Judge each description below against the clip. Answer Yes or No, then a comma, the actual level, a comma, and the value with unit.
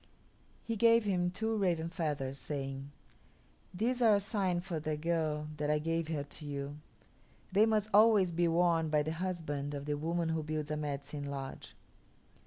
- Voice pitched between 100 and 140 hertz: No, medium, 160 Hz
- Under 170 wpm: No, average, 175 wpm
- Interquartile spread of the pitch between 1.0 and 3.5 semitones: No, average, 4.0 semitones